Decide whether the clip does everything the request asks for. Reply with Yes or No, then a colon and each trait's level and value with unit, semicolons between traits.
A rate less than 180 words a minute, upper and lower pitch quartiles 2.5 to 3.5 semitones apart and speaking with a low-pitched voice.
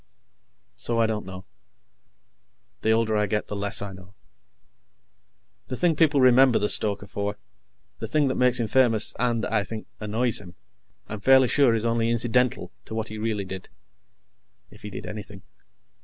Yes: average, 170 wpm; average, 3.1 semitones; low, 110 Hz